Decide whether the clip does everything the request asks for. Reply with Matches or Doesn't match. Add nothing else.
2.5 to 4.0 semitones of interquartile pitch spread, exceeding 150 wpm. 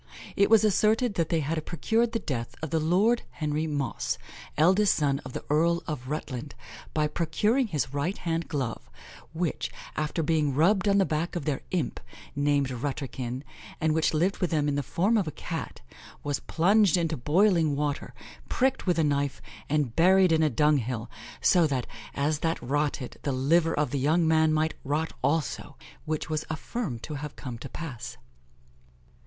Matches